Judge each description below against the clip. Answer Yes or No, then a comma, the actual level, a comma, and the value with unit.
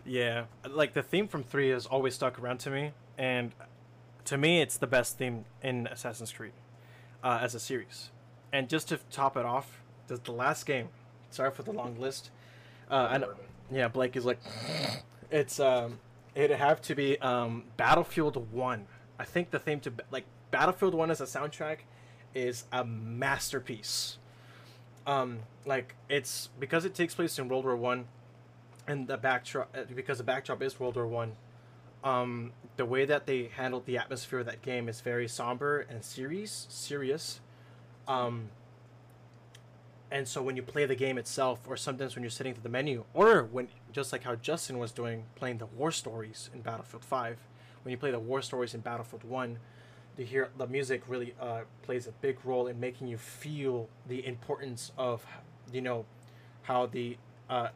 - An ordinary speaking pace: Yes, average, 175 wpm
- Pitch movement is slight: Yes, narrow, 1.8 semitones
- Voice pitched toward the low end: Yes, low, 125 Hz